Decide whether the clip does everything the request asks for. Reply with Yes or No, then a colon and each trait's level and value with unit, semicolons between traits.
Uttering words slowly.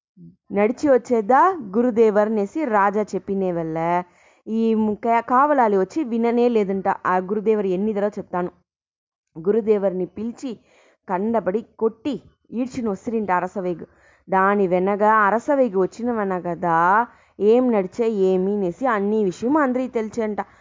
Yes: slow, 105 wpm